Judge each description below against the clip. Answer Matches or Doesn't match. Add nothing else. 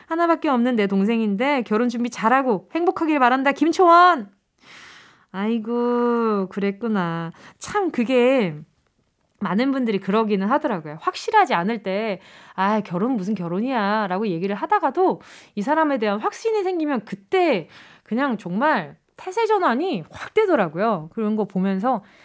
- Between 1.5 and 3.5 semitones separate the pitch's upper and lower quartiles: Doesn't match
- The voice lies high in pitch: Matches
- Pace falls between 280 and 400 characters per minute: Matches